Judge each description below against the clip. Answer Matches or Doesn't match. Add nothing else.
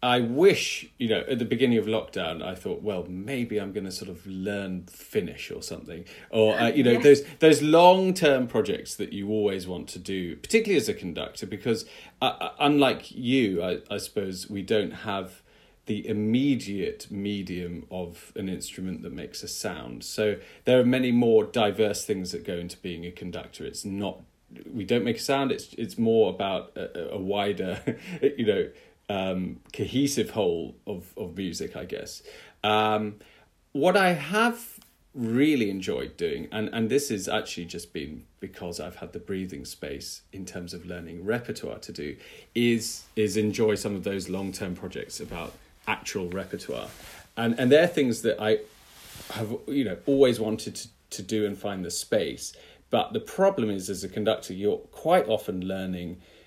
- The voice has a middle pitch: Doesn't match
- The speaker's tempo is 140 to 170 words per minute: Doesn't match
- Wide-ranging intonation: Matches